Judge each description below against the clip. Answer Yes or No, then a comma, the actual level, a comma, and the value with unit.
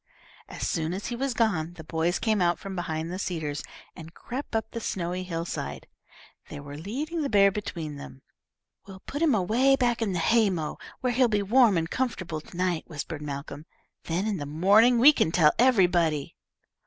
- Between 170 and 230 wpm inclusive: Yes, average, 190 wpm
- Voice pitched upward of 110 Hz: Yes, medium, 185 Hz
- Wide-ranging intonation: Yes, wide, 6.1 semitones